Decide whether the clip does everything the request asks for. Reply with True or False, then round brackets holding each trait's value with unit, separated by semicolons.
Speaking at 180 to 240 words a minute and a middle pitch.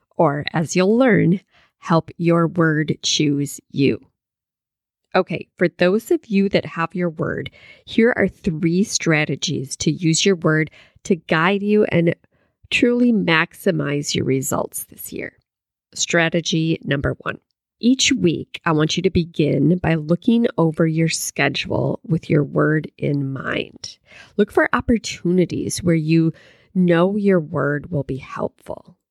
False (140 wpm; 170 Hz)